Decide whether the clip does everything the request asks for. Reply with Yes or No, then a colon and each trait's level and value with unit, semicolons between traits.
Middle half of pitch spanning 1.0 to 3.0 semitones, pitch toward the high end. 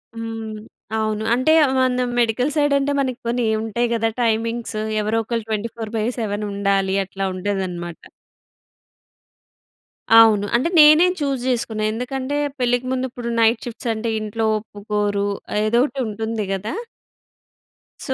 Yes: average, 2.7 semitones; high, 225 Hz